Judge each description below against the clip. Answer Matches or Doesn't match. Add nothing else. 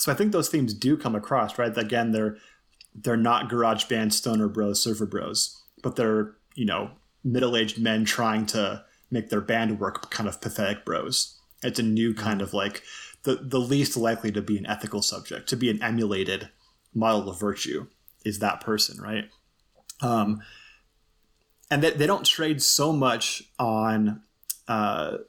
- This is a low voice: Matches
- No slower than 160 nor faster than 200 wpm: Matches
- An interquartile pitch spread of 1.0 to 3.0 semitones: Matches